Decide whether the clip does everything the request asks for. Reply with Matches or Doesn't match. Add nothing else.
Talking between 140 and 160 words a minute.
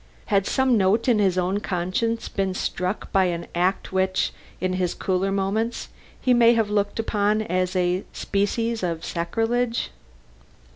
Matches